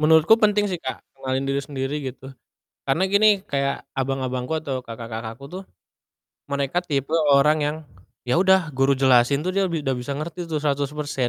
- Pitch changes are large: No, average, 2.9 semitones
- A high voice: No, medium, 140 Hz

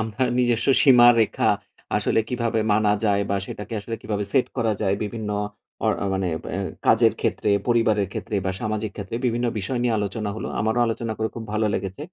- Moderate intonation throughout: No, narrow, 2.1 semitones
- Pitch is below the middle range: Yes, low, 110 Hz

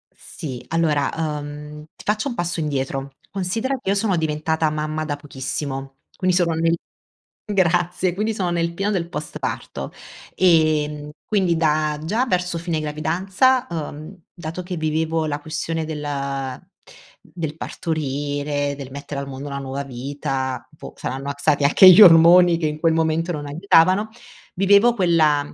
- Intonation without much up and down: No, average, 3.4 semitones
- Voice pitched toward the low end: No, medium, 160 Hz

